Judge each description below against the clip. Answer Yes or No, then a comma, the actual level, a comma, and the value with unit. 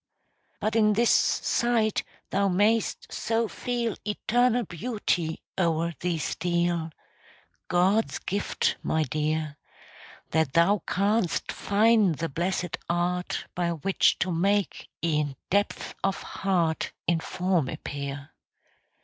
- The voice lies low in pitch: No, medium, 180 Hz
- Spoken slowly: Yes, slow, 110 wpm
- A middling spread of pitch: Yes, average, 4.2 semitones